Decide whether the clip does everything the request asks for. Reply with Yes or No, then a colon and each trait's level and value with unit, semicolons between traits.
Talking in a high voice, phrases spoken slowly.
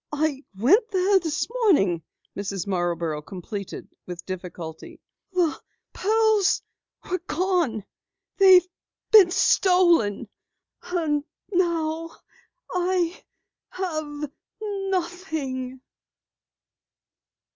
Yes: very high, 325 Hz; slow, 70 wpm